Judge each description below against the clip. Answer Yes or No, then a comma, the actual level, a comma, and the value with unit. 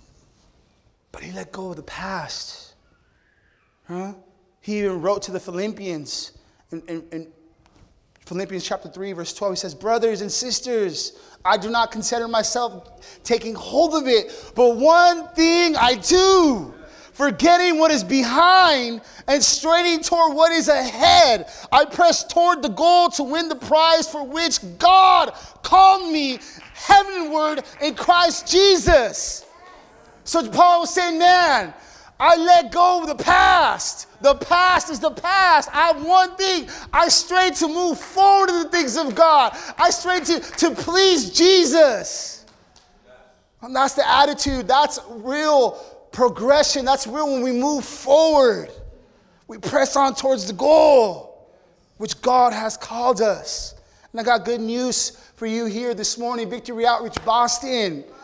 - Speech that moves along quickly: No, average, 145 wpm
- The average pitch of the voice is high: Yes, very high, 290 Hz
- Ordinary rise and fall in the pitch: No, wide, 6.7 semitones